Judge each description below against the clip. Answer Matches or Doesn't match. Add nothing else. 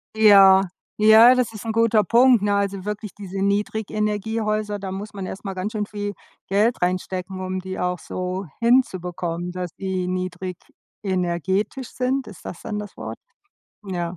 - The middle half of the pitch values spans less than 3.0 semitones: Matches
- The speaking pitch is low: Doesn't match